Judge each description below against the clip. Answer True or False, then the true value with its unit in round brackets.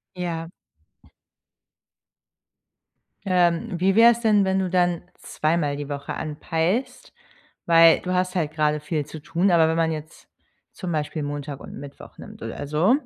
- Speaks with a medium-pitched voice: True (165 Hz)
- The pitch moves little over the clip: False (3.3 semitones)